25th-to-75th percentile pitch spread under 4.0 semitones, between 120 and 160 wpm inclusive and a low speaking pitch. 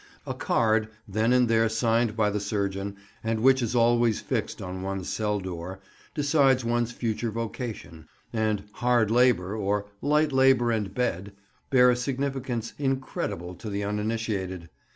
Yes: average, 3.4 semitones; average, 150 wpm; low, 115 Hz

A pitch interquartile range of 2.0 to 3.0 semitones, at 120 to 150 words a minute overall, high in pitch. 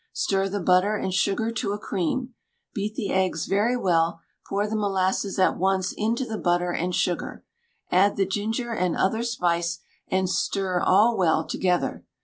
No: average, 2.7 semitones; average, 165 wpm; high, 195 Hz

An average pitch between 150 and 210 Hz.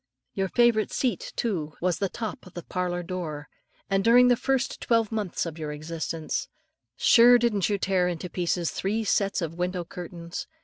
Yes: medium, 185 Hz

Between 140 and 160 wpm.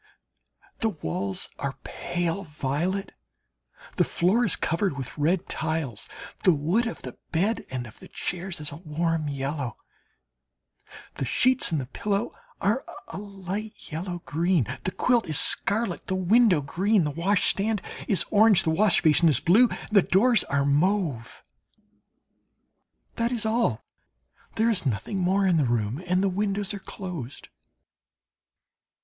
Yes: average, 145 wpm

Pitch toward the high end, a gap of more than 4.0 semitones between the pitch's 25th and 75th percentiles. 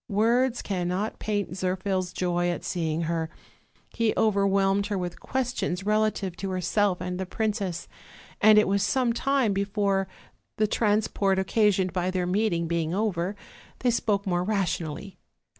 No: high, 195 Hz; average, 2.9 semitones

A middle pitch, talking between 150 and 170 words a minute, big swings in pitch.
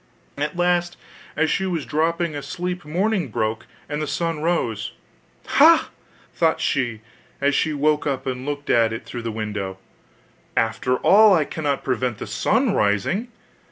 Yes: medium, 145 Hz; average, 155 wpm; wide, 6.5 semitones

